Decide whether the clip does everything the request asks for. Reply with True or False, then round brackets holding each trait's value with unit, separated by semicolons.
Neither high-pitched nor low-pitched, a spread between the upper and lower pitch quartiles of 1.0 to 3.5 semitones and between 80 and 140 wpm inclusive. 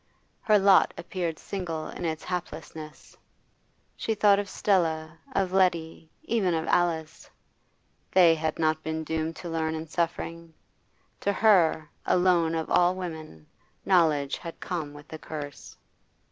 True (165 Hz; 2.4 semitones; 135 wpm)